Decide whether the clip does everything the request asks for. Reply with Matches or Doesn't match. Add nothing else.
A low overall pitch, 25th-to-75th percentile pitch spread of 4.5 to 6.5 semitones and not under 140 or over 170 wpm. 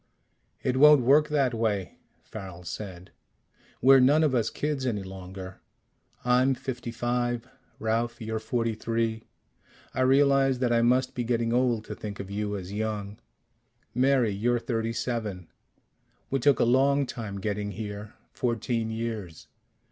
Doesn't match